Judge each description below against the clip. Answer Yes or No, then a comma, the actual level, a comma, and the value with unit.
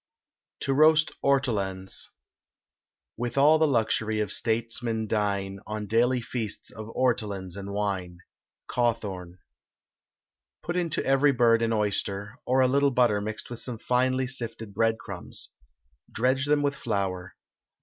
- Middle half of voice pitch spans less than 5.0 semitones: Yes, average, 4.0 semitones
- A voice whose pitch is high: No, low, 115 Hz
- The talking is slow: Yes, slow, 130 wpm